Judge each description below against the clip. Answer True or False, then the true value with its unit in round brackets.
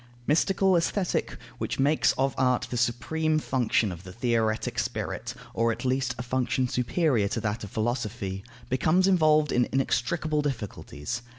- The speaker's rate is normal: True (150 wpm)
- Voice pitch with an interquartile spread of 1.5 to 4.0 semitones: False (4.8 semitones)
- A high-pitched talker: False (125 Hz)